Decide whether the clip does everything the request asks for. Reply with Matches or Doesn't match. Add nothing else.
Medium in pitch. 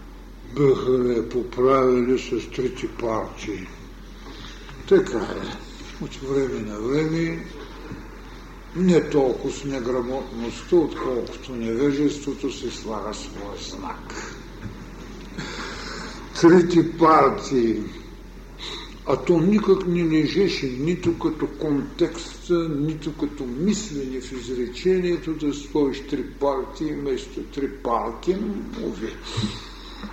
Matches